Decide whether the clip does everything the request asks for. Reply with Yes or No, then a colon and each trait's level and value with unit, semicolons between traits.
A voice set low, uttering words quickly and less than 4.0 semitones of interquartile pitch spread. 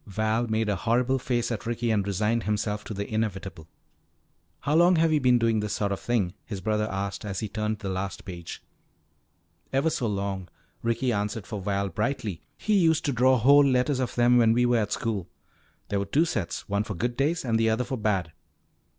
Yes: low, 110 Hz; fast, 210 wpm; average, 3.5 semitones